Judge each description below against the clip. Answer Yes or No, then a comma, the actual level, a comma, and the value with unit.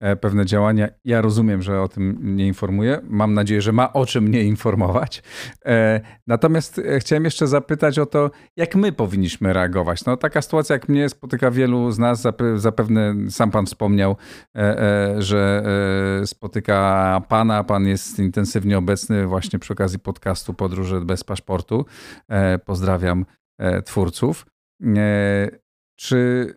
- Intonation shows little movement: No, average, 3.7 semitones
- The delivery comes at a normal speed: Yes, average, 130 wpm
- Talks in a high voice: No, low, 105 Hz